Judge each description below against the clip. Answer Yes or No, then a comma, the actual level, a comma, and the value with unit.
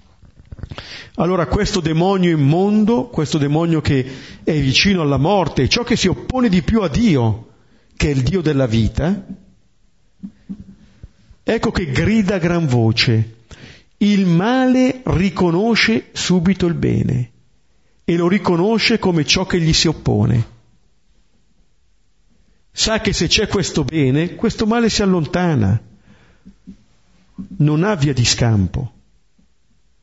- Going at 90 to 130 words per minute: Yes, average, 120 wpm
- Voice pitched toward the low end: No, medium, 170 Hz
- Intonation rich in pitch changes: Yes, wide, 7.2 semitones